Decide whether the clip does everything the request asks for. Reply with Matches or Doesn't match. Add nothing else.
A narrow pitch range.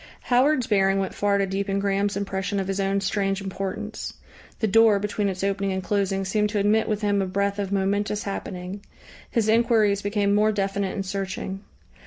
Matches